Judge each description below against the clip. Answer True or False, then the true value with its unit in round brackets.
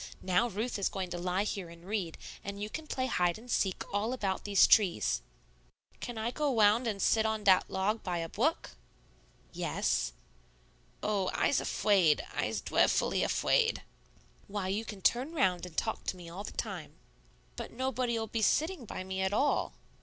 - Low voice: False (205 Hz)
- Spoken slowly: False (175 wpm)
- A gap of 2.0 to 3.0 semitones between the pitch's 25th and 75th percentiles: False (3.9 semitones)